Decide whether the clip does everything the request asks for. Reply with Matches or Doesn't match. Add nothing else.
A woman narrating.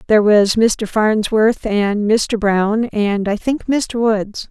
Matches